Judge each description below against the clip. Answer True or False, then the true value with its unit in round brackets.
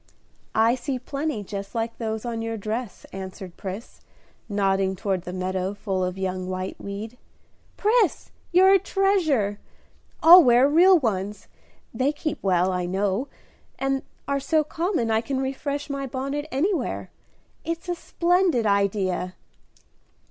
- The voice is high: True (230 Hz)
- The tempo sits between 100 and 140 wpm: True (135 wpm)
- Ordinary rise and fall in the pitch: False (7.1 semitones)